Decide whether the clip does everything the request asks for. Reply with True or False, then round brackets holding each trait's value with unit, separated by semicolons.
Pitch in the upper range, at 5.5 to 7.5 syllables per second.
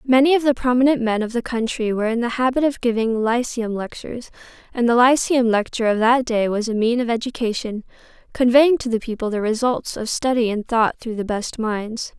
True (235 Hz; 5.6 syllables/s)